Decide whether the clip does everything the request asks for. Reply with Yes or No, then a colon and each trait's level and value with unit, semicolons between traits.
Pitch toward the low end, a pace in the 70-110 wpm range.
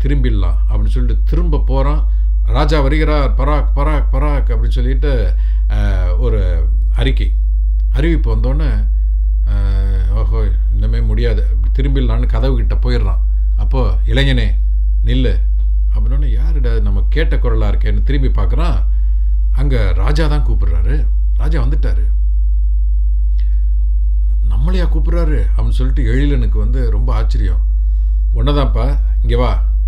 Yes: very low, 95 Hz; average, 100 wpm